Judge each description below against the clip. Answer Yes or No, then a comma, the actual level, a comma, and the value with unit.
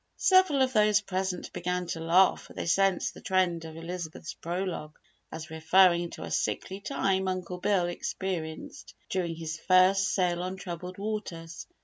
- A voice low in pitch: No, medium, 180 Hz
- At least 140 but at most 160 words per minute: Yes, average, 155 wpm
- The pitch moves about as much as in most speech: No, narrow, 2.3 semitones